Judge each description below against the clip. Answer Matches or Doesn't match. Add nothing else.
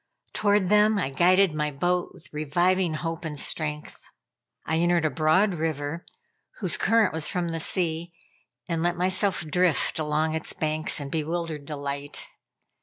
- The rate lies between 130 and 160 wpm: Matches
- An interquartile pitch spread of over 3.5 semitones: Doesn't match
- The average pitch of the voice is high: Doesn't match